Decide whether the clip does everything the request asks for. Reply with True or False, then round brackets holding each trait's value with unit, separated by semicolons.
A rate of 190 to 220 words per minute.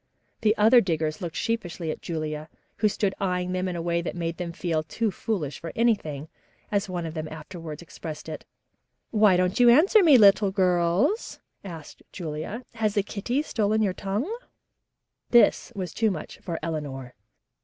False (170 wpm)